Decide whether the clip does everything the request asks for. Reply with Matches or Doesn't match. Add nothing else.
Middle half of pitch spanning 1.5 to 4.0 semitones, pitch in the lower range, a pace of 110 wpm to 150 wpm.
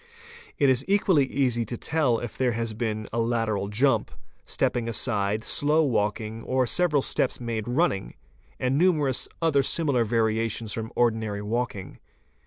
Matches